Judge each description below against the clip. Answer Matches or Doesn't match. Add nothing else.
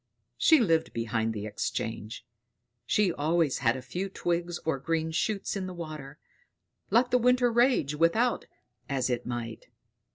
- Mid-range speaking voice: Matches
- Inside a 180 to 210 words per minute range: Doesn't match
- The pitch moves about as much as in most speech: Doesn't match